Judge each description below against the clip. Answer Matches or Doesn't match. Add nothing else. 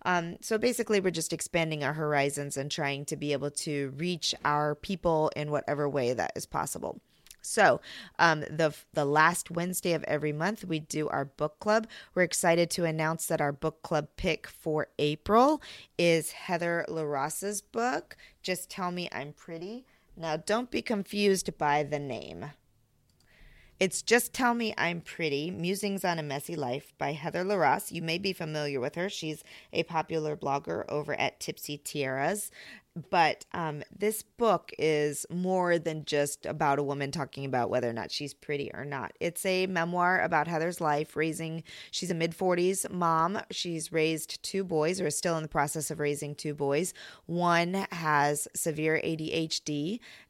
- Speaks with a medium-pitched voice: Matches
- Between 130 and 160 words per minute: Doesn't match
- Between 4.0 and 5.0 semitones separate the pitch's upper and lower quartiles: Doesn't match